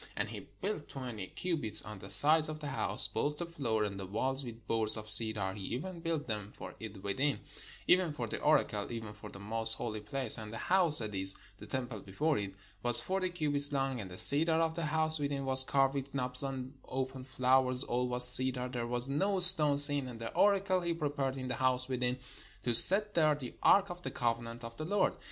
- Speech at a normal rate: No, fast, 220 wpm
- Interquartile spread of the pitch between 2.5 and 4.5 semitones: No, average, 5.1 semitones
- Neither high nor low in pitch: No, low, 130 Hz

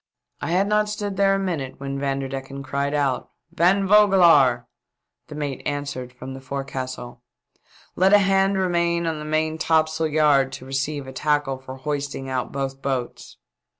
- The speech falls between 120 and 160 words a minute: No, average, 170 wpm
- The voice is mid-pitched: Yes, medium, 145 Hz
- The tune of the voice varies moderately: Yes, average, 4.3 semitones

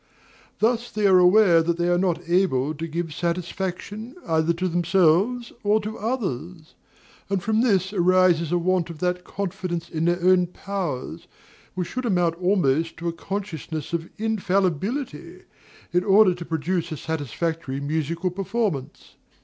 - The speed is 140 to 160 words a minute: Yes, average, 150 wpm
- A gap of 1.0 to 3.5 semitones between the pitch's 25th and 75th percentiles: Yes, average, 3.0 semitones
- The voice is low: No, medium, 180 Hz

